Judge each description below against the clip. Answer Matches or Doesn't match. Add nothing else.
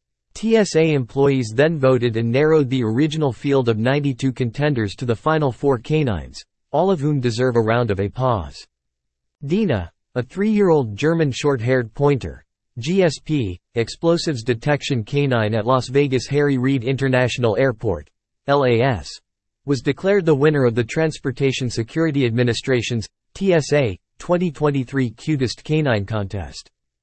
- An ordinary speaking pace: Doesn't match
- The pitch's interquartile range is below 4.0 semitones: Doesn't match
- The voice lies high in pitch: Doesn't match